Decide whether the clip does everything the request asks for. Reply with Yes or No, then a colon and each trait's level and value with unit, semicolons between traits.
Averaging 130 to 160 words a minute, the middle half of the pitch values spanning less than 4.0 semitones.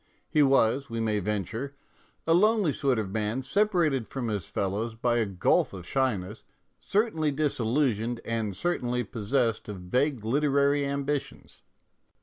No: average, 140 wpm; average, 4.6 semitones